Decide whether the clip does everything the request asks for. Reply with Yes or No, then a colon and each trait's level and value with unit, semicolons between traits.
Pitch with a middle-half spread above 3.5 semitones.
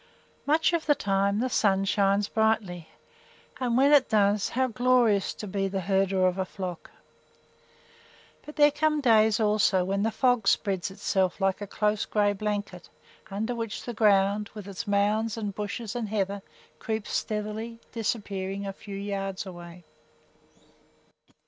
No: narrow, 2.4 semitones